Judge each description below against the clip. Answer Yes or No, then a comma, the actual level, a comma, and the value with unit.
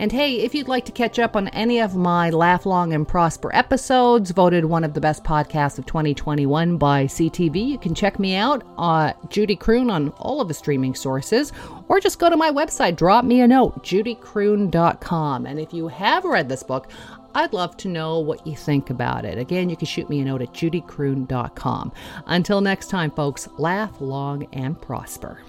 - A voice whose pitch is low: No, medium, 170 Hz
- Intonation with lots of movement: Yes, wide, 6.2 semitones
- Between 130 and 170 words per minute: No, average, 200 wpm